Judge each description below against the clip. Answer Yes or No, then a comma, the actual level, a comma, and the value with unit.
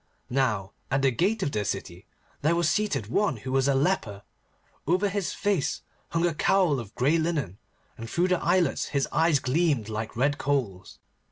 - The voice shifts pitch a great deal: Yes, wide, 7.0 semitones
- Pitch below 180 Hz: Yes, medium, 140 Hz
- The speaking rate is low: No, average, 180 wpm